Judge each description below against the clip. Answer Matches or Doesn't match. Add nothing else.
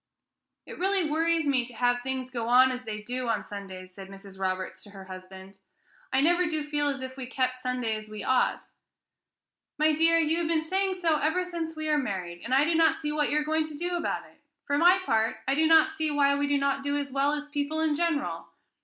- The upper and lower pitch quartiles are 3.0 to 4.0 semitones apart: Doesn't match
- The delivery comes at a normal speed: Doesn't match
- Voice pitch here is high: Matches